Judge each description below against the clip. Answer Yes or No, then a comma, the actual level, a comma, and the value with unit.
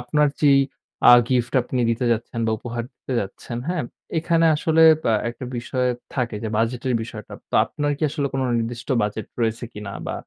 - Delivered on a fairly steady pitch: No, average, 3.5 semitones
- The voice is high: No, low, 120 Hz